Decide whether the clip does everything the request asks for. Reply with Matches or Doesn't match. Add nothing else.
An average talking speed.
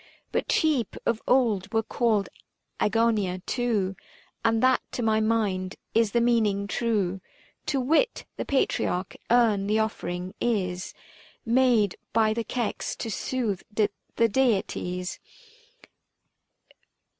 Doesn't match